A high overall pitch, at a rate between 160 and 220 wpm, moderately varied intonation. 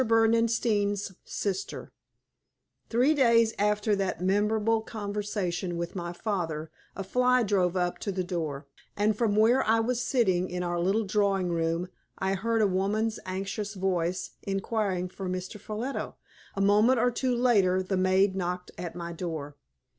No: high, 200 Hz; average, 150 wpm; average, 3.4 semitones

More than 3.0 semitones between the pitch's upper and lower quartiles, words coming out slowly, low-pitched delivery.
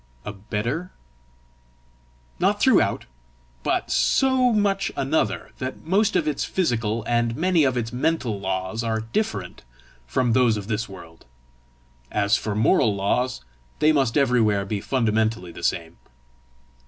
Yes: average, 5.1 semitones; slow, 130 wpm; low, 115 Hz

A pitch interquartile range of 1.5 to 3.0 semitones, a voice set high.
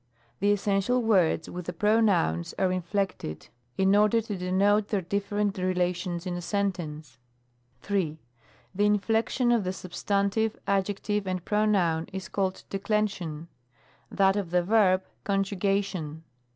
Yes: narrow, 2.5 semitones; high, 195 Hz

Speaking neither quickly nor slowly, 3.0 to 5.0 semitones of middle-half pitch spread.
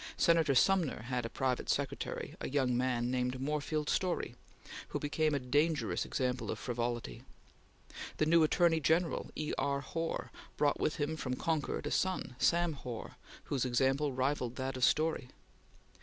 Yes: average, 155 wpm; average, 3.8 semitones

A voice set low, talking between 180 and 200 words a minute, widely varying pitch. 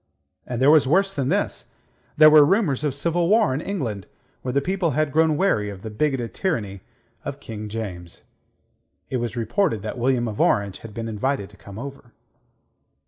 Yes: low, 130 Hz; average, 185 wpm; wide, 6.0 semitones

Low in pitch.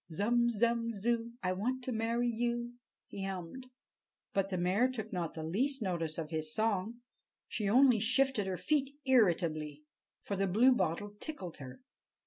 No: high, 215 Hz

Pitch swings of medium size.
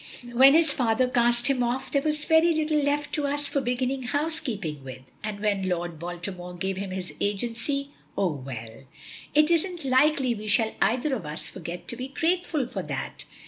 No: wide, 7.3 semitones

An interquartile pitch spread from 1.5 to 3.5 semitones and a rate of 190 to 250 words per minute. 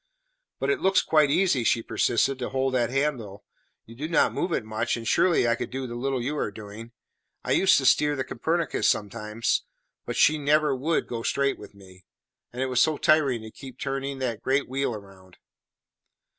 No: average, 4.1 semitones; average, 200 wpm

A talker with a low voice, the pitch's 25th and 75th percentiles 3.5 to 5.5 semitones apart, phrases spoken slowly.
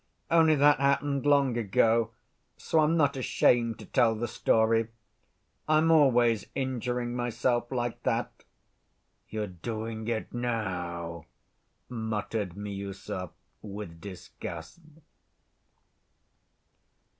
Yes: low, 115 Hz; average, 4.0 semitones; slow, 95 wpm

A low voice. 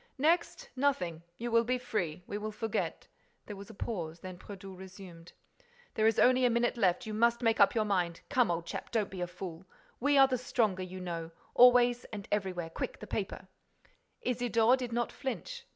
No: high, 215 Hz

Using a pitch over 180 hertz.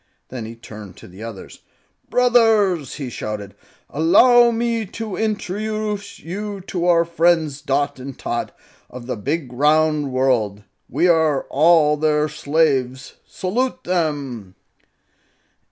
No: medium, 155 Hz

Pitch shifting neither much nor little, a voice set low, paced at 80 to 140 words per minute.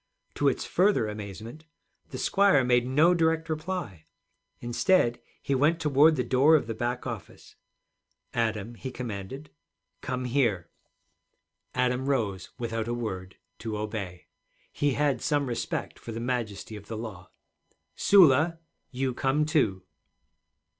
Yes: average, 5.0 semitones; low, 125 Hz; slow, 135 wpm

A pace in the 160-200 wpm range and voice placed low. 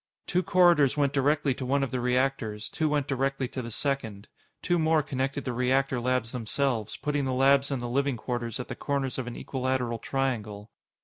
Yes: average, 195 wpm; low, 130 Hz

